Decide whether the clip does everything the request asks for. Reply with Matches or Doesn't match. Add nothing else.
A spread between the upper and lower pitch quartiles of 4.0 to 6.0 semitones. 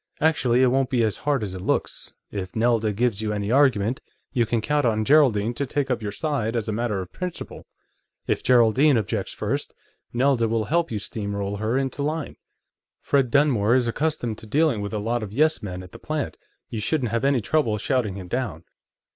Matches